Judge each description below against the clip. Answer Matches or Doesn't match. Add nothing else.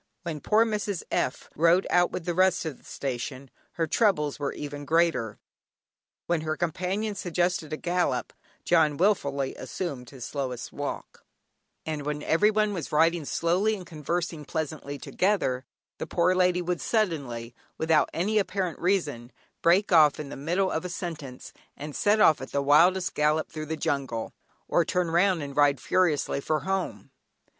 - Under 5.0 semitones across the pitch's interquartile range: Matches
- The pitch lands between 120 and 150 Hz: Doesn't match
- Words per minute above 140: Matches